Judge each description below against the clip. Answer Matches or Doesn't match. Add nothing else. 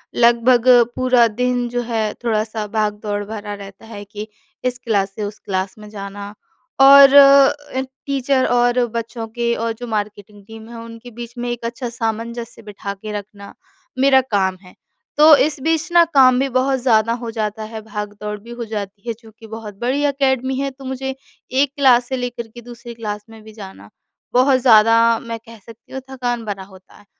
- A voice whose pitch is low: Doesn't match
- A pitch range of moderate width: Matches